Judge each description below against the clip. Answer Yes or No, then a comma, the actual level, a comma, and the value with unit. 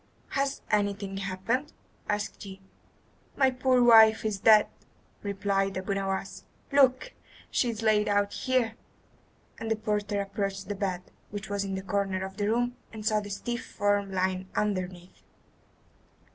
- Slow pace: No, average, 145 wpm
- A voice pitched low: No, high, 205 Hz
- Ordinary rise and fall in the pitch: No, narrow, 2.3 semitones